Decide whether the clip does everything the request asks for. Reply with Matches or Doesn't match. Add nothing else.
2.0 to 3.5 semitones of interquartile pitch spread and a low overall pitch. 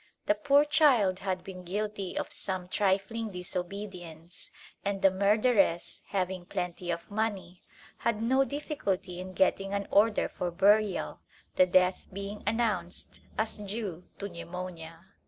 Doesn't match